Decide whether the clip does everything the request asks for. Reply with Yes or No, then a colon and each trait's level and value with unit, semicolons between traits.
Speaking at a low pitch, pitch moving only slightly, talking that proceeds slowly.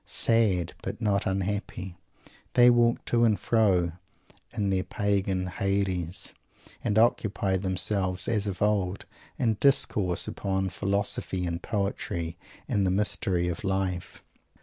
Yes: very low, 95 Hz; narrow, 2.2 semitones; slow, 125 wpm